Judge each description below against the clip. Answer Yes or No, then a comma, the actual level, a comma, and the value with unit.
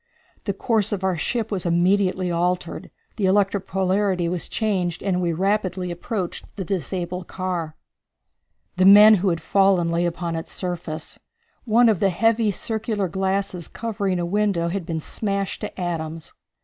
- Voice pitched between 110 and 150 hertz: No, medium, 185 Hz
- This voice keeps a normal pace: Yes, average, 155 wpm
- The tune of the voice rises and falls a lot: No, narrow, 2.6 semitones